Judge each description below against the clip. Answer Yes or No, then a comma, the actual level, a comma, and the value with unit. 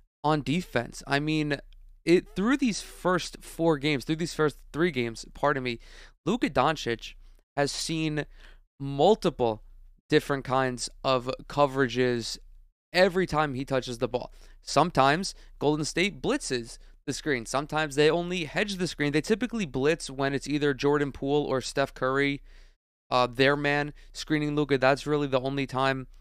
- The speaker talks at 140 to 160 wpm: Yes, average, 150 wpm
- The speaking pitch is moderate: Yes, medium, 145 Hz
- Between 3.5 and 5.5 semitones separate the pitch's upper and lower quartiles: No, average, 2.9 semitones